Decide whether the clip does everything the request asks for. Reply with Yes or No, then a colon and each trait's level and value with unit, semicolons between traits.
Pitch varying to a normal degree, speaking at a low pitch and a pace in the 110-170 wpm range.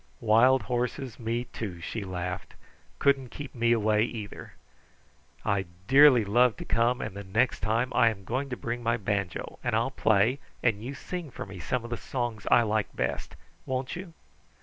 No: average, 3.3 semitones; low, 115 Hz; average, 180 wpm